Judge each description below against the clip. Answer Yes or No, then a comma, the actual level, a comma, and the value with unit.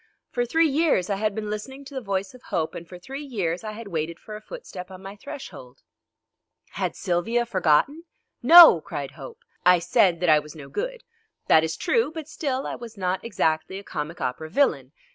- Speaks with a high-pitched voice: Yes, high, 205 Hz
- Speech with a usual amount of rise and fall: No, wide, 7.7 semitones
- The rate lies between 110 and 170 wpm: No, average, 200 wpm